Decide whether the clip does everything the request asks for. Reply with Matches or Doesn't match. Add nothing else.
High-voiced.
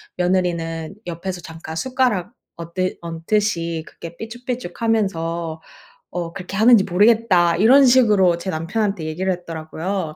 Doesn't match